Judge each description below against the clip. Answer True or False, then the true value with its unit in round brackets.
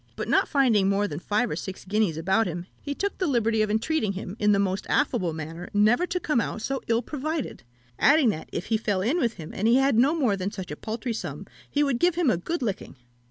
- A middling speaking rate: False (250 wpm)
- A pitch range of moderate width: False (6.0 semitones)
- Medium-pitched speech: False (220 Hz)